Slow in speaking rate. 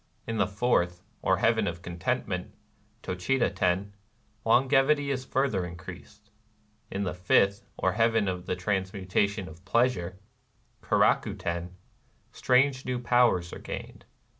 Yes: slow, 125 wpm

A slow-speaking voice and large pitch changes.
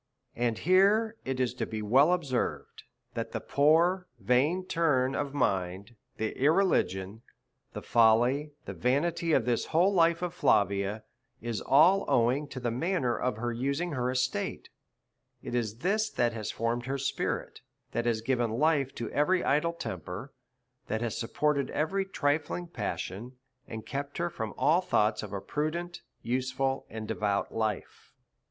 No: average, 155 wpm; wide, 6.1 semitones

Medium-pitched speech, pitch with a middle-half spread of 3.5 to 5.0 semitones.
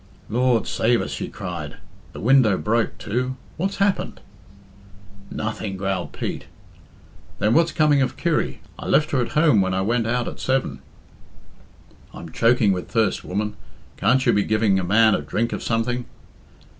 No: low, 115 Hz; average, 4.2 semitones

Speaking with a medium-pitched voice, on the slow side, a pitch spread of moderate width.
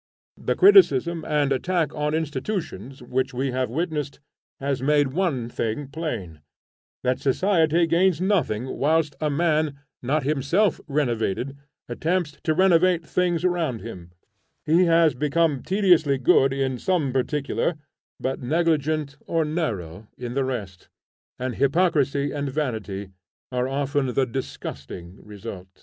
Yes: medium, 145 Hz; slow, 130 wpm; average, 4.4 semitones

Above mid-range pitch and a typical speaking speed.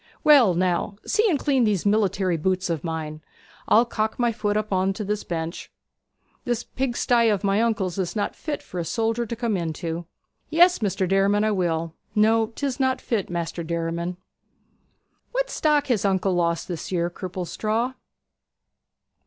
Yes: high, 200 Hz; average, 160 wpm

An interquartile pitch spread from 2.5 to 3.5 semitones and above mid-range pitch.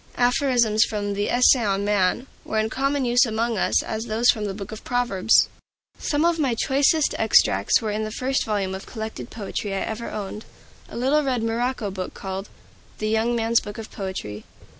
Yes: average, 3.1 semitones; high, 220 Hz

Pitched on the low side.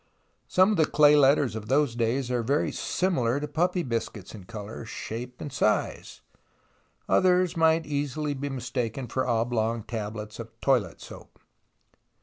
Yes: low, 125 Hz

